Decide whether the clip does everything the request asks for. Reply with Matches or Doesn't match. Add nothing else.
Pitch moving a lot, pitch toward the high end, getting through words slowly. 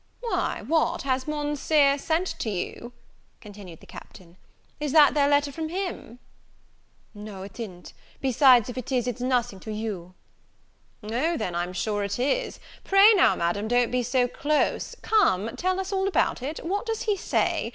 Doesn't match